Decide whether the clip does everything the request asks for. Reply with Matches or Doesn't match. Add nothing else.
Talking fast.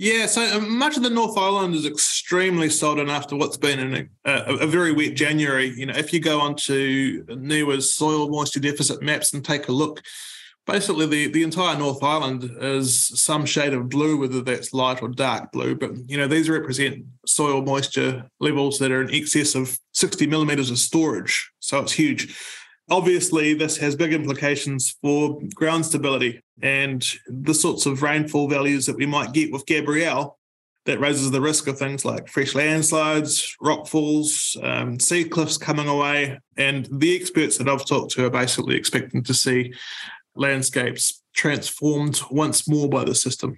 Doesn't match